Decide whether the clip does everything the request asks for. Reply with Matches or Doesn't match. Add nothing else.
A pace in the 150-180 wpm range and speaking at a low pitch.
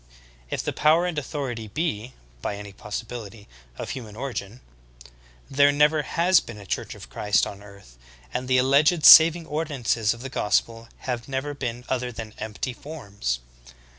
Matches